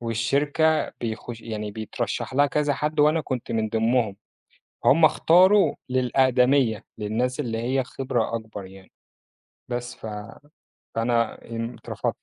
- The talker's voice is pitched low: Yes, low, 120 Hz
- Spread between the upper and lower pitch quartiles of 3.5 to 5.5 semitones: Yes, average, 3.8 semitones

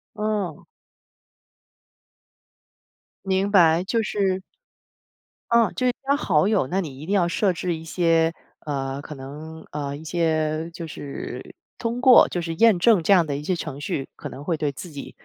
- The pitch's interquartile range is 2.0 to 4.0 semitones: No, average, 4.5 semitones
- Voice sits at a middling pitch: Yes, medium, 165 Hz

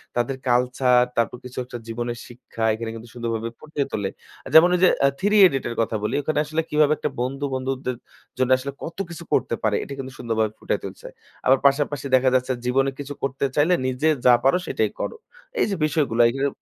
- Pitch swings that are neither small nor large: Yes, average, 3.0 semitones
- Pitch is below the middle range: Yes, low, 130 Hz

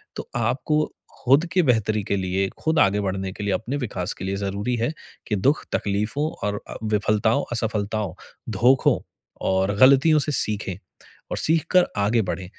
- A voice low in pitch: Yes, low, 110 Hz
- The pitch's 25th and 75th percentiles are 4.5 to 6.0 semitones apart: Yes, average, 4.8 semitones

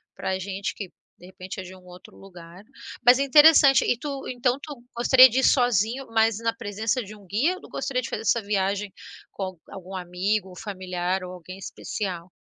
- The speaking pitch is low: No, high, 205 Hz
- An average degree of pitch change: Yes, average, 4.7 semitones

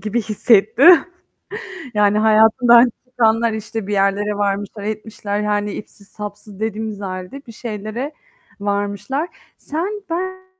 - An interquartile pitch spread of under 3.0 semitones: Yes, narrow, 2.4 semitones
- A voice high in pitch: Yes, high, 215 Hz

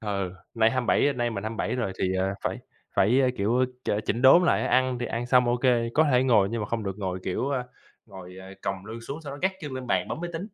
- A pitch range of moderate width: Yes, average, 4.6 semitones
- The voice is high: No, low, 120 Hz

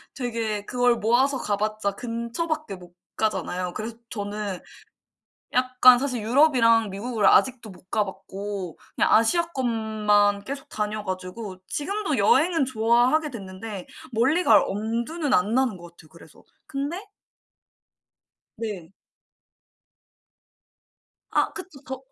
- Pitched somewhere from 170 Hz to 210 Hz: No, high, 225 Hz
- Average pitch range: Yes, average, 4.3 semitones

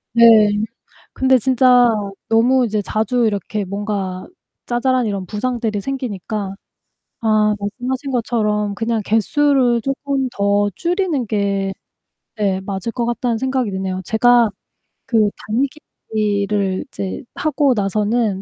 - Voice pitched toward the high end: Yes, high, 220 Hz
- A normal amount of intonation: Yes, average, 3.6 semitones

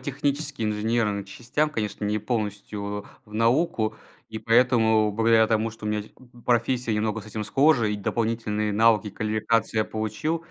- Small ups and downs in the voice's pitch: Yes, narrow, 2.0 semitones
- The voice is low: Yes, low, 110 Hz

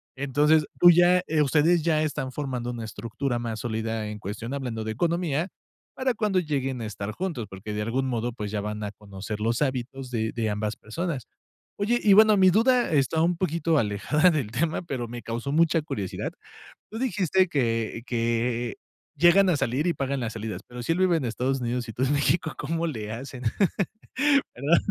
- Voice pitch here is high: No, low, 130 Hz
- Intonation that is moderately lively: No, wide, 6.4 semitones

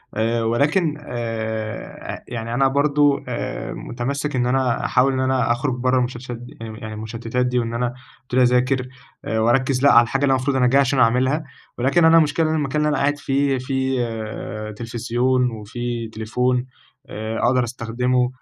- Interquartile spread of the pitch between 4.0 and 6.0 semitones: No, narrow, 2.4 semitones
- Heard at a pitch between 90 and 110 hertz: No, low, 125 Hz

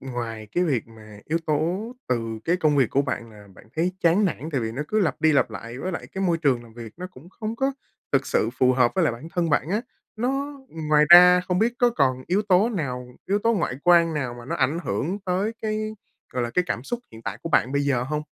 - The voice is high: No, medium, 155 Hz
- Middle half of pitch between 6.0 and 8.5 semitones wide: Yes, wide, 6.7 semitones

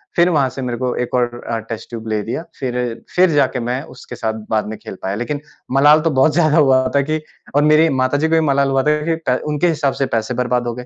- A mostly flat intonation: No, average, 3.6 semitones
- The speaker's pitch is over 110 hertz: Yes, low, 135 Hz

